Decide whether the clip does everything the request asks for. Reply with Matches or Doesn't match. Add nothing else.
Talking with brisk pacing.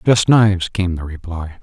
Doesn't match